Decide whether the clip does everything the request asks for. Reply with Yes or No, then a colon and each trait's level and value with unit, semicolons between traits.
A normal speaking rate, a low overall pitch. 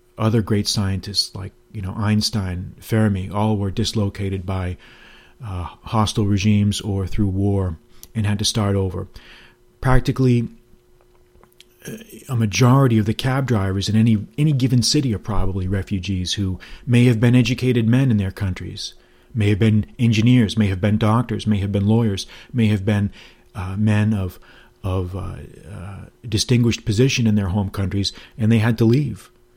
Yes: average, 160 wpm; low, 105 Hz